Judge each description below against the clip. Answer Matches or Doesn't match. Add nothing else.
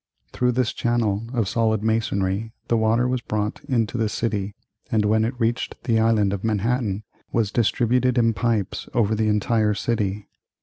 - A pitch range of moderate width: Doesn't match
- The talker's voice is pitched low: Matches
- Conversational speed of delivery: Matches